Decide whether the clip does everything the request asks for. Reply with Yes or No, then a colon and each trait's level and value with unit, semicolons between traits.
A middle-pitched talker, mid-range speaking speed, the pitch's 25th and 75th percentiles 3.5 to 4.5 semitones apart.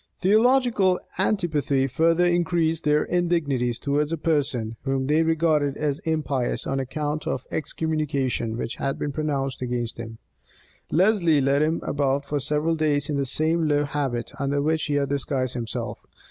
No: medium, 150 Hz; average, 160 wpm; average, 3.0 semitones